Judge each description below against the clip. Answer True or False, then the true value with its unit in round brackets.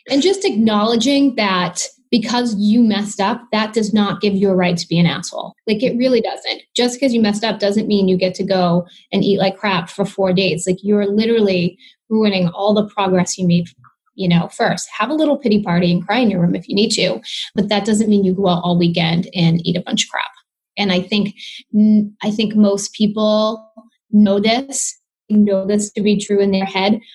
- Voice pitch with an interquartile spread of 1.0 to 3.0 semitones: True (2.7 semitones)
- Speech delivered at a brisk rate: True (220 wpm)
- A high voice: True (205 Hz)